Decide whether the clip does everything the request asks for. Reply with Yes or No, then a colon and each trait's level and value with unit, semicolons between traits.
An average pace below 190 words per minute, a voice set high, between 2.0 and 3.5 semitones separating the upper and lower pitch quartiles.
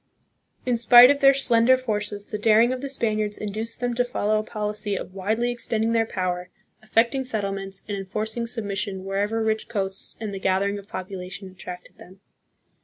Yes: average, 180 wpm; high, 215 Hz; average, 2.9 semitones